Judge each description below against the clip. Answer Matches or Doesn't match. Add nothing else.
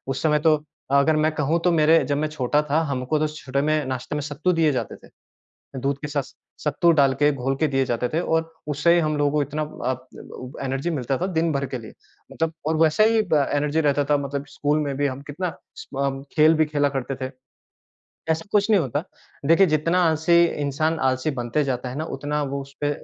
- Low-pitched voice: Doesn't match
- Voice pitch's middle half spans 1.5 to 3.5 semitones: Matches